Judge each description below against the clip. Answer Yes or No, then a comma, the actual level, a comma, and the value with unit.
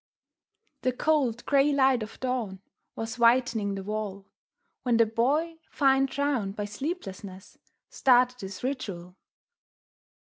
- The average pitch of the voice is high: Yes, high, 240 Hz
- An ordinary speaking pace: No, slow, 115 wpm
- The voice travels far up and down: No, average, 4.7 semitones